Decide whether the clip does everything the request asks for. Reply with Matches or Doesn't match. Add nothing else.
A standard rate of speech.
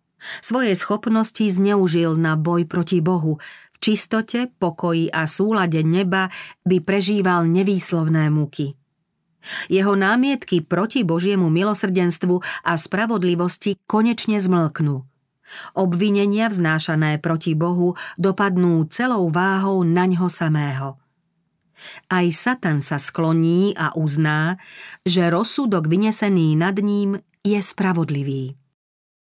Doesn't match